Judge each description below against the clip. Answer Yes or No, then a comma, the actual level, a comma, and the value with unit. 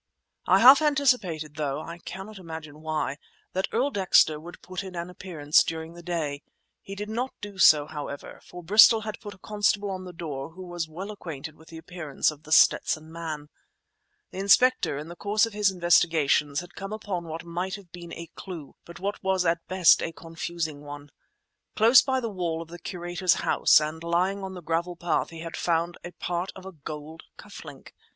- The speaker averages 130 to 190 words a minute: No, average, 200 wpm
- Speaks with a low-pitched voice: No, medium, 175 Hz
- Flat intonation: No, average, 3.4 semitones